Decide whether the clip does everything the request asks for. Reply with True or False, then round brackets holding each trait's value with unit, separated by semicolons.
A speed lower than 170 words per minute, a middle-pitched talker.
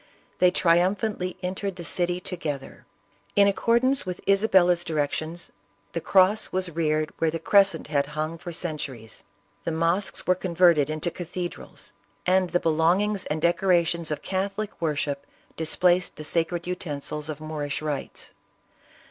True (140 wpm; 170 Hz)